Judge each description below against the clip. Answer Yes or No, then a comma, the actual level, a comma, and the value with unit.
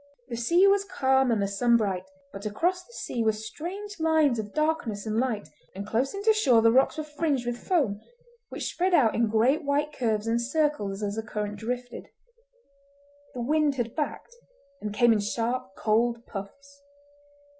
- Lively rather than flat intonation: Yes, wide, 5.8 semitones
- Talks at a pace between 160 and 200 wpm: Yes, average, 180 wpm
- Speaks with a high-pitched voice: Yes, high, 240 Hz